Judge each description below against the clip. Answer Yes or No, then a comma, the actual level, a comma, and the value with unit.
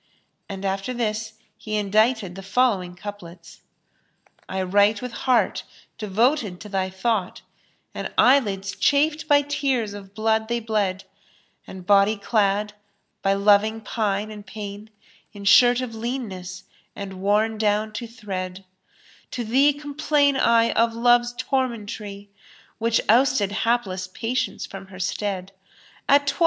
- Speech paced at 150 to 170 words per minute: No, average, 140 wpm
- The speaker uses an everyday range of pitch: Yes, average, 3.4 semitones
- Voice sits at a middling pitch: No, high, 215 Hz